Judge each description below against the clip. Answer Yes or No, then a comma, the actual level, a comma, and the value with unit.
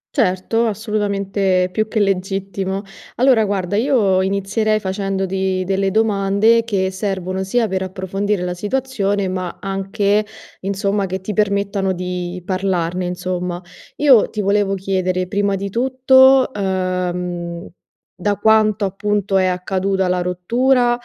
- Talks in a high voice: Yes, high, 195 Hz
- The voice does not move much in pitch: Yes, narrow, 2.1 semitones